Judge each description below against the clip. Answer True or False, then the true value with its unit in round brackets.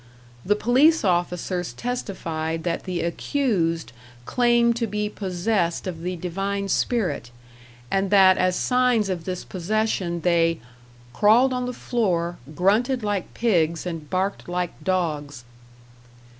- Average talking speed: False (125 wpm)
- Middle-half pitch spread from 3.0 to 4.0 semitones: False (4.5 semitones)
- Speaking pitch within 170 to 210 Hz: True (185 Hz)